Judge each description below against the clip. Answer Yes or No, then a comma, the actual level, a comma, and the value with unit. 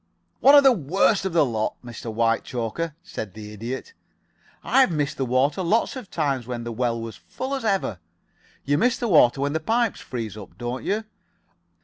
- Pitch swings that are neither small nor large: No, wide, 9.0 semitones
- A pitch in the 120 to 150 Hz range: Yes, medium, 140 Hz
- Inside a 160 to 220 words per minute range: Yes, average, 195 wpm